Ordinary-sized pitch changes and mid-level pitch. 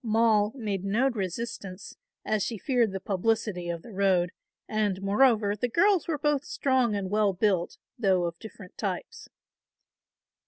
No: average, 3.6 semitones; high, 210 Hz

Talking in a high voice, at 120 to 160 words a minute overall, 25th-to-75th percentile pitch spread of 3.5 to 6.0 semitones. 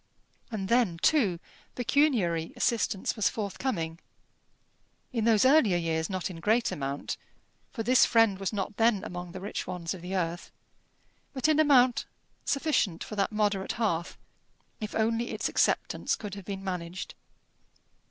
Yes: high, 200 Hz; average, 145 wpm; average, 4.7 semitones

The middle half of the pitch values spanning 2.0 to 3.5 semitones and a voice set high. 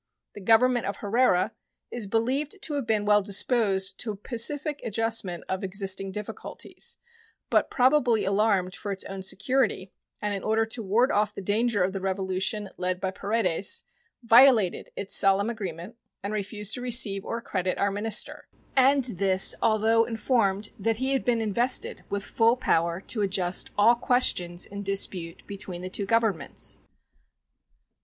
Yes: average, 3.2 semitones; high, 210 Hz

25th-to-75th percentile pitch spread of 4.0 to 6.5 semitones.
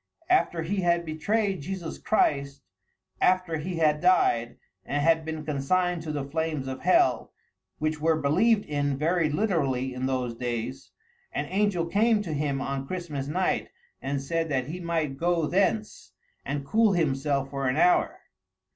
Yes: average, 4.4 semitones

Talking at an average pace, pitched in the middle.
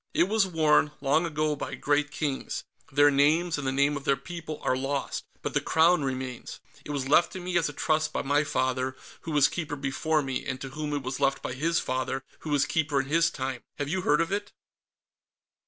No: fast, 220 wpm; medium, 145 Hz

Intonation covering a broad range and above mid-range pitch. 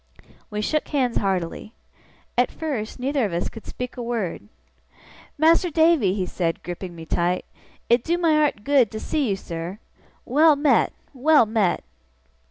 Yes: wide, 7.6 semitones; high, 235 Hz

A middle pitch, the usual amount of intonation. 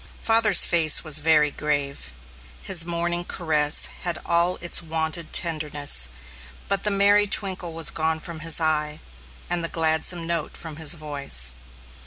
No: medium, 160 Hz; narrow, 2.3 semitones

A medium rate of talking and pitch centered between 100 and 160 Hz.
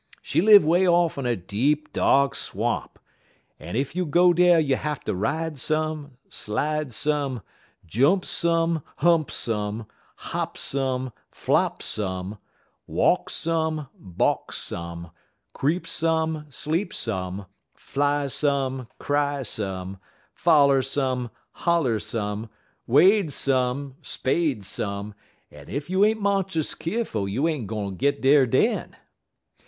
No: slow, 120 wpm; medium, 140 Hz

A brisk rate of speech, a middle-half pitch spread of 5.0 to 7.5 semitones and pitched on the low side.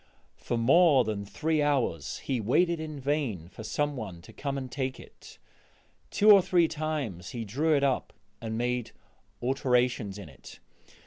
No: average, 165 wpm; average, 5.3 semitones; low, 130 Hz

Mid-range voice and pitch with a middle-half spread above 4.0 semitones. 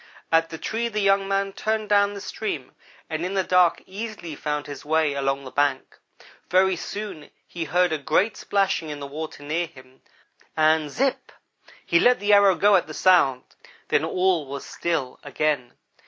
Yes: medium, 170 Hz; average, 5.1 semitones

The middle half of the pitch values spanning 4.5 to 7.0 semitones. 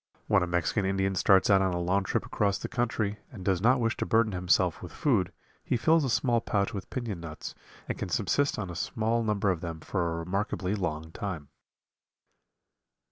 No: average, 3.9 semitones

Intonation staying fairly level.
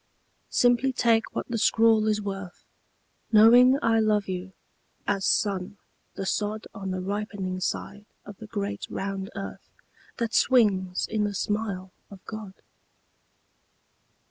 Yes: narrow, 2.3 semitones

